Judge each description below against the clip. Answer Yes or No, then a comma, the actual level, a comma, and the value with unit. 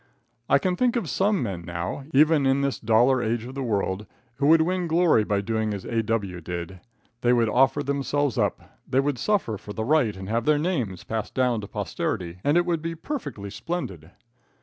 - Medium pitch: No, low, 125 Hz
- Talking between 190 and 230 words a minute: Yes, average, 200 wpm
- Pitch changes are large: Yes, wide, 6.5 semitones